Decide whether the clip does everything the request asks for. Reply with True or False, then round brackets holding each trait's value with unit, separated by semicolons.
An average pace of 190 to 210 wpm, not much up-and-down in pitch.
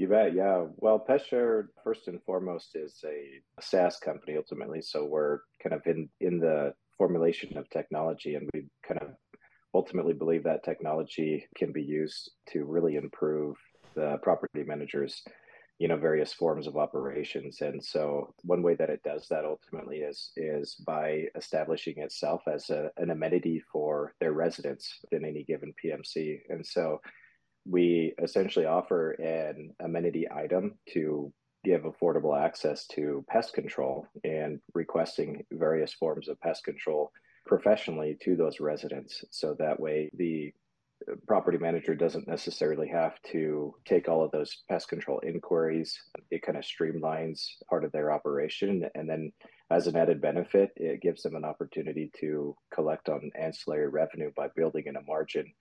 False (155 wpm; 2.1 semitones)